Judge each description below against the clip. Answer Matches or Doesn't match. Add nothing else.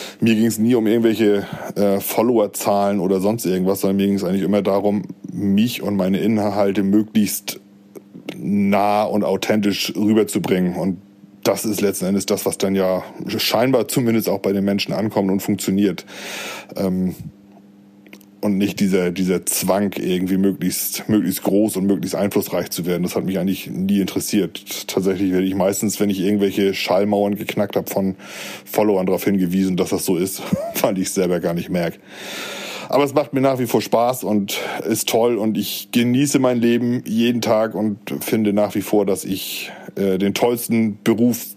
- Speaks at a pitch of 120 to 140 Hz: Doesn't match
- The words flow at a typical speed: Matches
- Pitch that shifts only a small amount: Matches